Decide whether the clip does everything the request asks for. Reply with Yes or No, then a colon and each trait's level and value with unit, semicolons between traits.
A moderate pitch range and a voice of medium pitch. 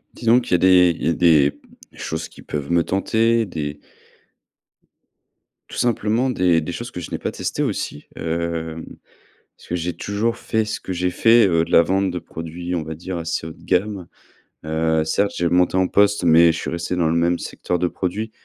No: average, 3.2 semitones; very low, 90 Hz